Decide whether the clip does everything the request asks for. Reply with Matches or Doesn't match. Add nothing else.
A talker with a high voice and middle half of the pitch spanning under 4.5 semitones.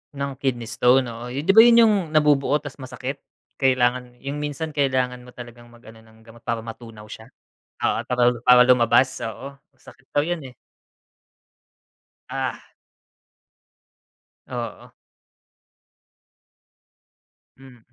Doesn't match